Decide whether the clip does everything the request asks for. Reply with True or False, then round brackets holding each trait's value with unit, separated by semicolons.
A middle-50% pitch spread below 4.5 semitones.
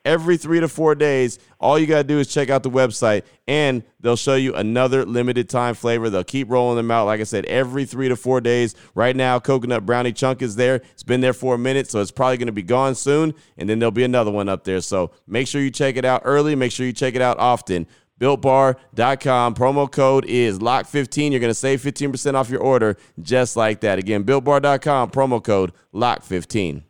True (2.5 semitones)